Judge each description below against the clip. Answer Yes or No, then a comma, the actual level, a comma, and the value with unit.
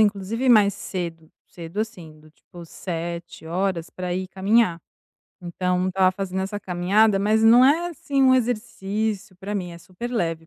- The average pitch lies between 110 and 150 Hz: No, high, 190 Hz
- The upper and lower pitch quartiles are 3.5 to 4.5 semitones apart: Yes, average, 3.8 semitones